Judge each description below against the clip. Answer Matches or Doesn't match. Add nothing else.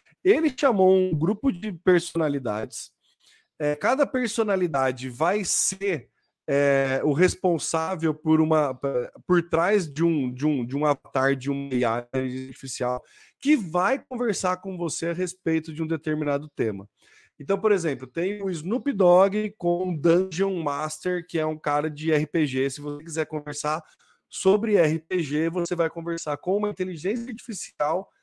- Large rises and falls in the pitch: Doesn't match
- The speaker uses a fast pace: Doesn't match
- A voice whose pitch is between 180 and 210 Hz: Doesn't match